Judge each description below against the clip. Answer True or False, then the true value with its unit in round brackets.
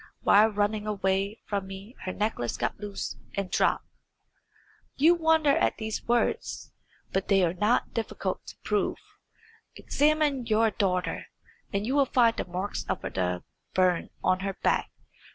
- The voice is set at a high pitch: True (205 Hz)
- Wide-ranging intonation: False (3.5 semitones)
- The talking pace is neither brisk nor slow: True (150 wpm)